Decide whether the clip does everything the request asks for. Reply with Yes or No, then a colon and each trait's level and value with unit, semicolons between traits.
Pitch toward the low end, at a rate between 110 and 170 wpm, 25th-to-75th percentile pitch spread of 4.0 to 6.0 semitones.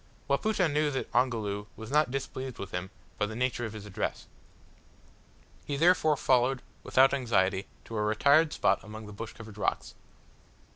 Yes: low, 120 Hz; average, 160 wpm; average, 4.8 semitones